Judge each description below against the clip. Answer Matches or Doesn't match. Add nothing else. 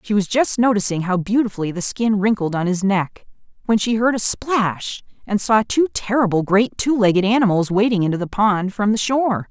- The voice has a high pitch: Matches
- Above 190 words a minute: Matches